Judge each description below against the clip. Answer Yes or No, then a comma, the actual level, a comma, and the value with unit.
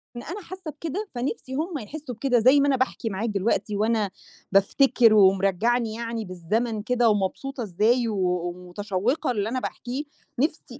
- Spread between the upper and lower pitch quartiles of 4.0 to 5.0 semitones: Yes, average, 4.6 semitones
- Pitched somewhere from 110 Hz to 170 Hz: No, high, 230 Hz